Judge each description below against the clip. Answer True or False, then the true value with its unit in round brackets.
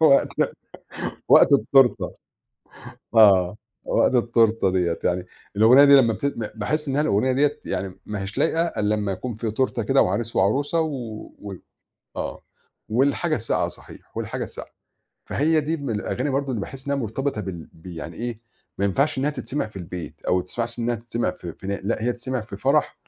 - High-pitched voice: False (115 Hz)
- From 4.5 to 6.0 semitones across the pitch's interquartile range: True (5.4 semitones)